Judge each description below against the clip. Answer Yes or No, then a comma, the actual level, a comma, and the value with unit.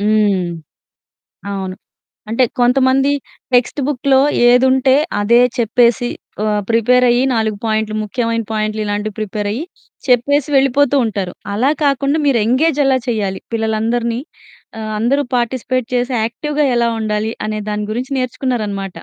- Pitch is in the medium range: No, high, 235 Hz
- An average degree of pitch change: Yes, average, 3.3 semitones